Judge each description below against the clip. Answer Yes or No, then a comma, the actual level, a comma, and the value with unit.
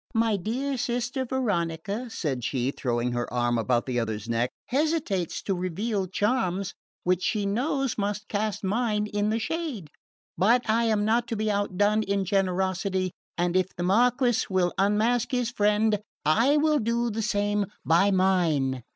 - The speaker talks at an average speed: Yes, average, 160 wpm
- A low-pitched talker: No, high, 205 Hz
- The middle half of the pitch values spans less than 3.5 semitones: No, average, 4.5 semitones